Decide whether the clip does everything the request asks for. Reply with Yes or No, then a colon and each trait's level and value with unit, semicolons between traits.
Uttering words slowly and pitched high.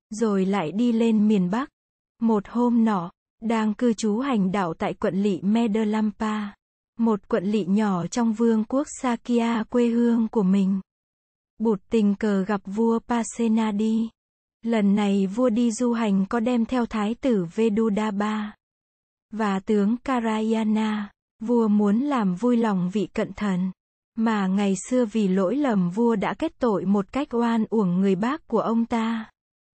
Yes: slow, 155 wpm; high, 220 Hz